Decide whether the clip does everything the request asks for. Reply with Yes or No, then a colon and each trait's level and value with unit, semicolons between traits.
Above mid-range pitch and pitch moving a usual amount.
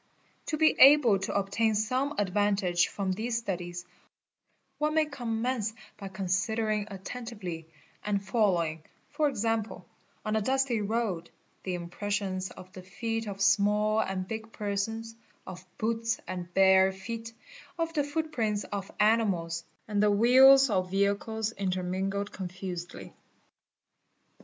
Yes: high, 205 Hz; average, 3.2 semitones